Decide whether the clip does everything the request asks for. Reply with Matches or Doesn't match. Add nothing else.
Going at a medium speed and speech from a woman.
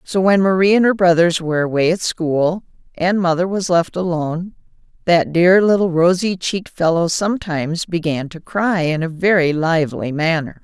Matches